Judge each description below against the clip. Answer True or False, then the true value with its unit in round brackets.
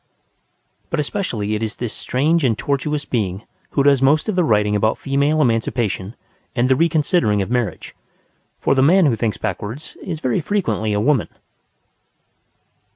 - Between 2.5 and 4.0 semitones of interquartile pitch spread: False (5.6 semitones)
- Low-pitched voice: True (130 Hz)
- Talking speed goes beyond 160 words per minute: False (155 wpm)